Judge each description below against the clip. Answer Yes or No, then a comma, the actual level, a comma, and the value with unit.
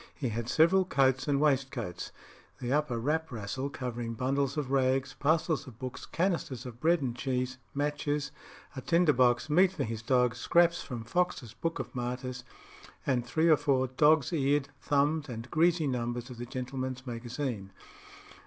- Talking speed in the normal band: Yes, average, 160 wpm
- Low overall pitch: Yes, low, 130 Hz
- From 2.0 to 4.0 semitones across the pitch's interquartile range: Yes, average, 3.4 semitones